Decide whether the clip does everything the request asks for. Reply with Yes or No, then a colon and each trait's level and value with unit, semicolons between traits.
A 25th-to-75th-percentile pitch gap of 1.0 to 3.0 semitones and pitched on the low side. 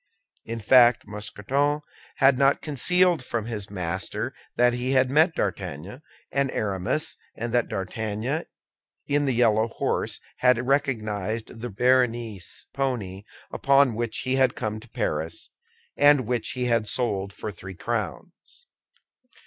No: average, 4.2 semitones; low, 120 Hz